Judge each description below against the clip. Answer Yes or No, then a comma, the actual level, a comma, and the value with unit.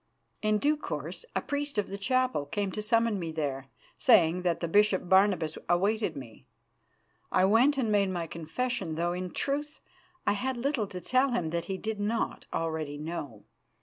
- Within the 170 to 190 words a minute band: Yes, average, 180 wpm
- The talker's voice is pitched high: Yes, high, 195 Hz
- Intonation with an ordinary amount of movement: No, wide, 5.7 semitones